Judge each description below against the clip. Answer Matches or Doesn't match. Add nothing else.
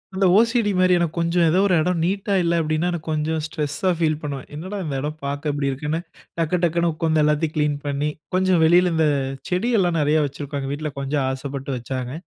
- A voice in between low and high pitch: Matches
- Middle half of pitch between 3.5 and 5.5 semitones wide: Doesn't match